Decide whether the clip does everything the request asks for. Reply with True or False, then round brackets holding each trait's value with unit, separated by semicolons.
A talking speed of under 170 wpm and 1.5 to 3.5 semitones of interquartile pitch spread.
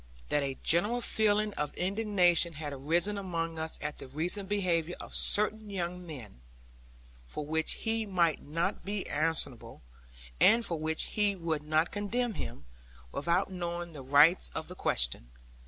False (155 wpm; 4.7 semitones)